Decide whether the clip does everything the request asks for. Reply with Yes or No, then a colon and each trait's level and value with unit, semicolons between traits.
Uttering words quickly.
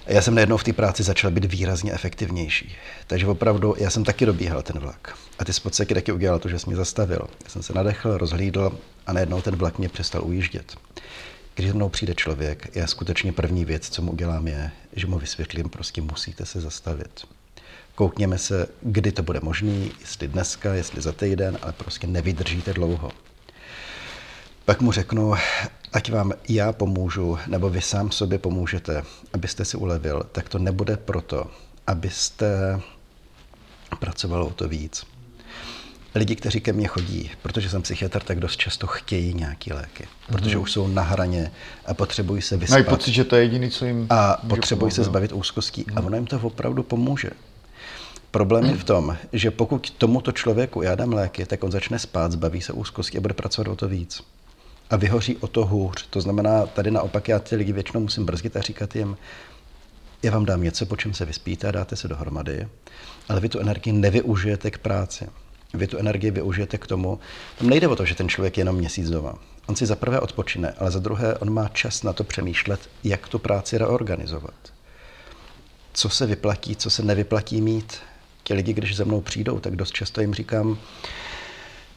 Yes: fast, 180 wpm